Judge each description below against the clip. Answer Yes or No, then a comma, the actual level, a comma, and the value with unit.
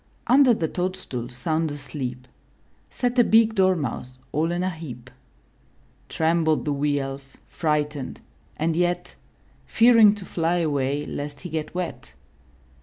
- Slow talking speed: Yes, slow, 130 wpm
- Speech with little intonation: No, average, 4.2 semitones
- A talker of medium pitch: Yes, medium, 160 Hz